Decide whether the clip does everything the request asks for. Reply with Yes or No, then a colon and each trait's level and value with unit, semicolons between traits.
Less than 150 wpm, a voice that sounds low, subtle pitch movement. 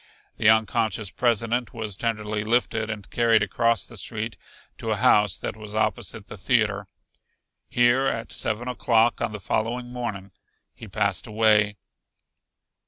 Yes: average, 140 wpm; low, 110 Hz; narrow, 2.0 semitones